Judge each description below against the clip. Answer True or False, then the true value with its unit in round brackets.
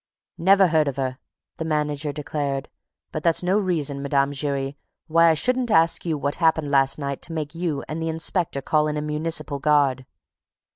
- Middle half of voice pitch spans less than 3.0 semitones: True (2.6 semitones)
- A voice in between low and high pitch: True (150 Hz)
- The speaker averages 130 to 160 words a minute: False (185 wpm)